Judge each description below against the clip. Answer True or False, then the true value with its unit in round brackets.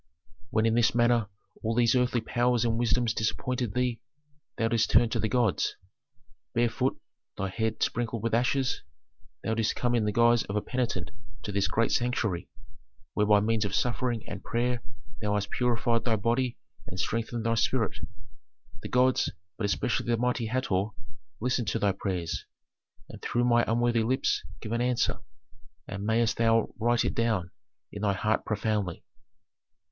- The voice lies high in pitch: False (115 Hz)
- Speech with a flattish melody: True (2.1 semitones)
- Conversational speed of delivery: True (165 wpm)